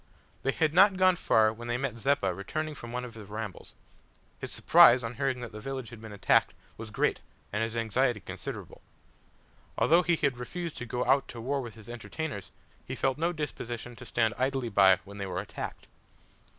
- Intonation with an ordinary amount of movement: Yes, average, 3.9 semitones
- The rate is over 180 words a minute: Yes, average, 200 wpm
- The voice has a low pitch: Yes, low, 120 Hz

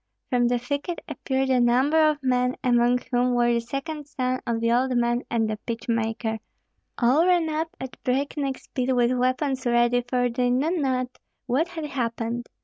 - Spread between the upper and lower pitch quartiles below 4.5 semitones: Yes, narrow, 2.4 semitones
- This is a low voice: No, very high, 250 Hz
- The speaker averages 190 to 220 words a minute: No, average, 180 wpm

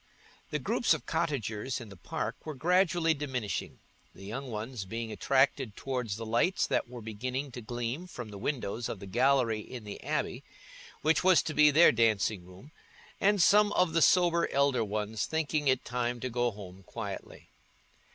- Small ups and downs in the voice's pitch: No, wide, 5.4 semitones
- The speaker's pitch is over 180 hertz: No, low, 125 Hz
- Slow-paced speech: No, average, 175 wpm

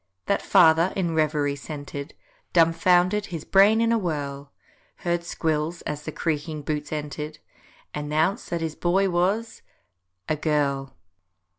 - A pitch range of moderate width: Yes, average, 3.0 semitones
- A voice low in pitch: No, medium, 160 Hz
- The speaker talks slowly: Yes, slow, 120 wpm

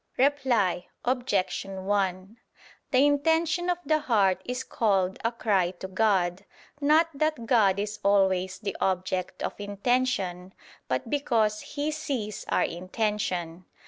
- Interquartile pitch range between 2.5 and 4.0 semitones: No, wide, 5.4 semitones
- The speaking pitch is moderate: No, high, 210 Hz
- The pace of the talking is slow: Yes, slow, 125 wpm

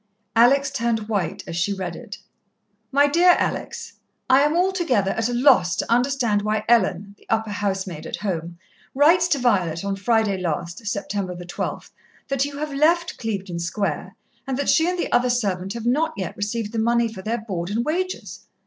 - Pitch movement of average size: No, wide, 6.0 semitones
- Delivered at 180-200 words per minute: Yes, average, 185 wpm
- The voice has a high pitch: Yes, high, 225 Hz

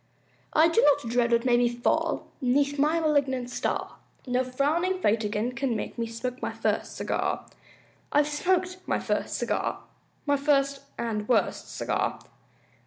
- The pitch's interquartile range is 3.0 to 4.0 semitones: Yes, average, 3.6 semitones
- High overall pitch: Yes, very high, 265 Hz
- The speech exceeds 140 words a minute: Yes, average, 150 wpm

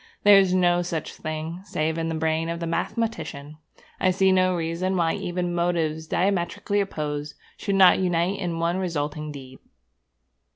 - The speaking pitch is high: No, medium, 170 Hz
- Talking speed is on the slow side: No, average, 160 wpm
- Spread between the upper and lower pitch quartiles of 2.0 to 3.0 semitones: Yes, average, 2.7 semitones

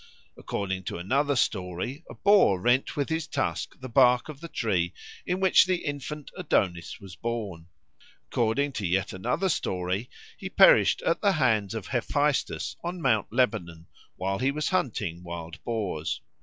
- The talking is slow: No, average, 155 wpm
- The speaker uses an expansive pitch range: Yes, wide, 7.8 semitones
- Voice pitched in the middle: No, low, 120 Hz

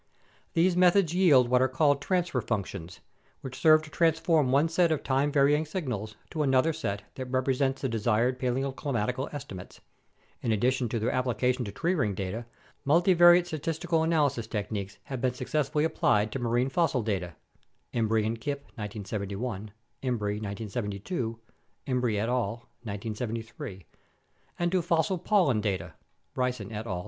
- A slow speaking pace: No, average, 150 wpm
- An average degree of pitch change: No, wide, 5.9 semitones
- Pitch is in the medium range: No, low, 125 Hz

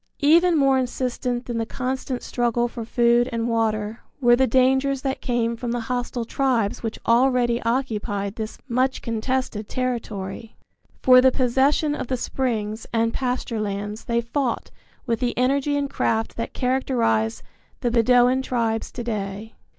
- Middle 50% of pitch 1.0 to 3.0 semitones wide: Yes, narrow, 2.4 semitones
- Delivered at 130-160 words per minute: Yes, average, 150 wpm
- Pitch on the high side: Yes, high, 240 Hz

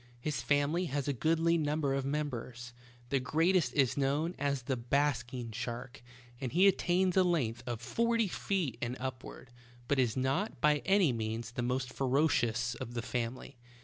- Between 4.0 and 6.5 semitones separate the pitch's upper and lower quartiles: Yes, average, 4.5 semitones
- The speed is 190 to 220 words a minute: No, average, 170 wpm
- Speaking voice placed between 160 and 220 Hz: No, low, 135 Hz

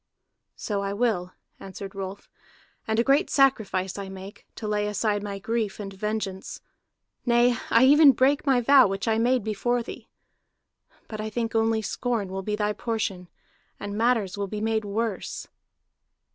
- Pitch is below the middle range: No, high, 215 Hz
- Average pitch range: Yes, average, 3.0 semitones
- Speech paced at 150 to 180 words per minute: Yes, average, 160 wpm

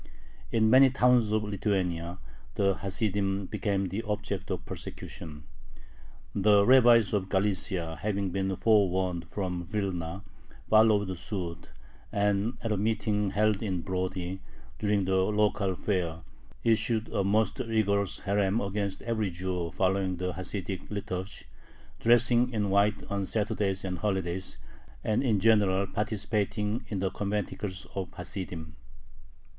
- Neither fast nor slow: No, slow, 130 wpm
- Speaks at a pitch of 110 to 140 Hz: No, low, 100 Hz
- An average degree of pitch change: No, narrow, 2.2 semitones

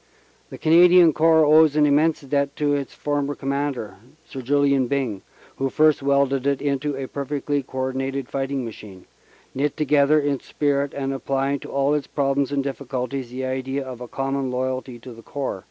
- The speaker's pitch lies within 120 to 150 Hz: Yes, medium, 140 Hz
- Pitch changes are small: Yes, narrow, 1.6 semitones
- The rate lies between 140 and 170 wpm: No, average, 180 wpm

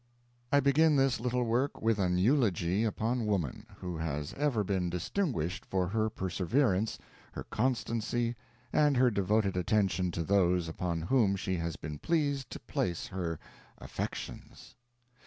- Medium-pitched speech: No, low, 105 Hz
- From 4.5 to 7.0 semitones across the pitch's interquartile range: Yes, wide, 5.6 semitones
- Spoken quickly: No, average, 140 wpm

